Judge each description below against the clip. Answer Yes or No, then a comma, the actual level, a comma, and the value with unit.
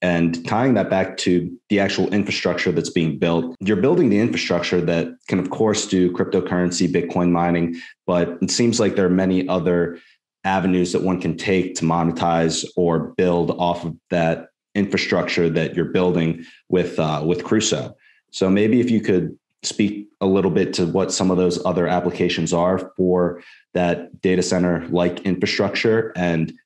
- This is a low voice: Yes, very low, 90 Hz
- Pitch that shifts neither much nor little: No, narrow, 1.8 semitones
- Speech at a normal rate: Yes, average, 170 wpm